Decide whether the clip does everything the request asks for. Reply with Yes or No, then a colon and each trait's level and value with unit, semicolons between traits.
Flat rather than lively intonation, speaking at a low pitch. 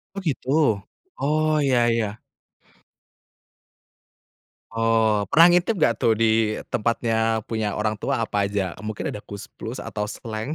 Yes: narrow, 2.3 semitones; low, 110 Hz